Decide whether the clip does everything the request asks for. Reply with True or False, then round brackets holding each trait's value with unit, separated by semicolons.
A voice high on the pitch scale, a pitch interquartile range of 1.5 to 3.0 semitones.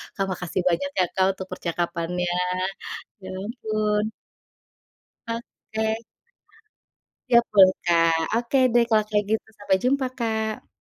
False (210 Hz; 3.7 semitones)